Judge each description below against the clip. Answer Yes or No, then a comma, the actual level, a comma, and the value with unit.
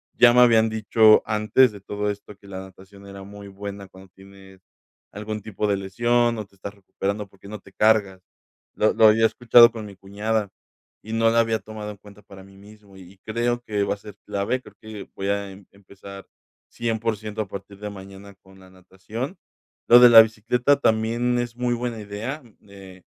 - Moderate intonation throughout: No, narrow, 2.3 semitones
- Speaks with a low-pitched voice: Yes, low, 105 Hz